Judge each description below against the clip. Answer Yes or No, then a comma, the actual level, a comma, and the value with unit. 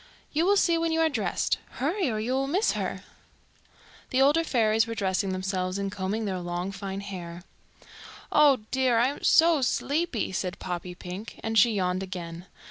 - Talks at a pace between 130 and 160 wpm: No, average, 180 wpm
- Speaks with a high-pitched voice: Yes, high, 215 Hz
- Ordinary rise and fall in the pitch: No, wide, 6.7 semitones